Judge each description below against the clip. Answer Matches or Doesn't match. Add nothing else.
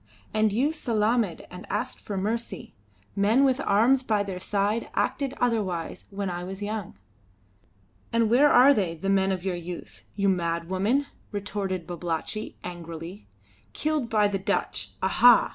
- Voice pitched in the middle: Doesn't match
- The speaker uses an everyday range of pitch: Matches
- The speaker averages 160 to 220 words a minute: Doesn't match